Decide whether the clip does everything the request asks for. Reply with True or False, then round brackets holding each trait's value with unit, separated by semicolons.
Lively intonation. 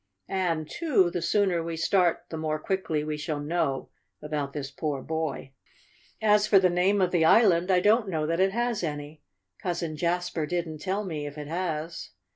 False (3.6 semitones)